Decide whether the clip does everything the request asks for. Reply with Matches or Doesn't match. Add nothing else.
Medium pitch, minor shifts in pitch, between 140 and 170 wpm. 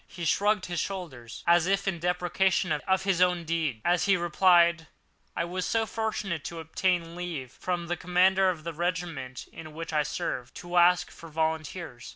Doesn't match